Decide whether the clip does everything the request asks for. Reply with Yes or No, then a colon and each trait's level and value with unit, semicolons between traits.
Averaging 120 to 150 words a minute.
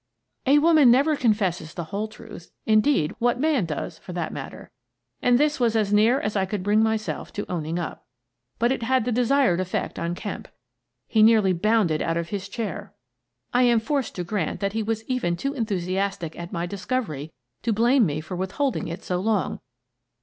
No: average, 200 wpm